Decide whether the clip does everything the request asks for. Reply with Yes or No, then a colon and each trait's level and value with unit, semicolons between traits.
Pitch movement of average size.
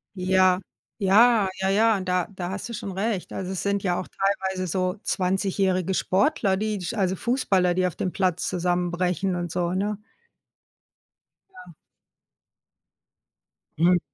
No: narrow, 1.8 semitones